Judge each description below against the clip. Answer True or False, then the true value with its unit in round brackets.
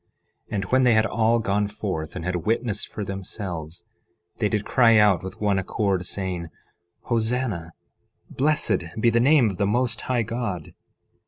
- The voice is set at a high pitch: False (105 Hz)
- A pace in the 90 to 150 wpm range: False (170 wpm)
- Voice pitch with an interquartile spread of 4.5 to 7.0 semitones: False (3.8 semitones)